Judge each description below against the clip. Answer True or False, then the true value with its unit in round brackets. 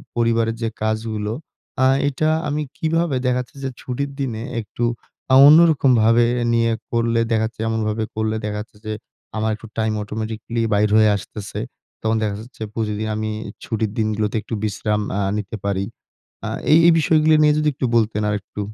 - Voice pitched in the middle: False (110 Hz)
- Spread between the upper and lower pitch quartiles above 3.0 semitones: False (2.7 semitones)